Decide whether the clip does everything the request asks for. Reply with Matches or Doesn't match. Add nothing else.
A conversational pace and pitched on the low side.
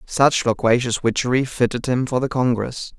Matches